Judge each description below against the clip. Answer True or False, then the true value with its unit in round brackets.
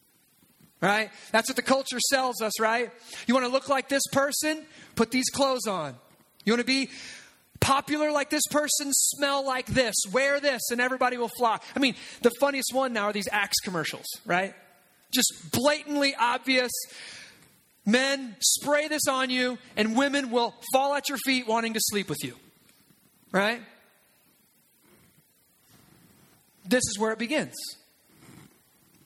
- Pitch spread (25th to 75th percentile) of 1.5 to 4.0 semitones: True (3.6 semitones)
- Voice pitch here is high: True (255 Hz)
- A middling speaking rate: True (150 wpm)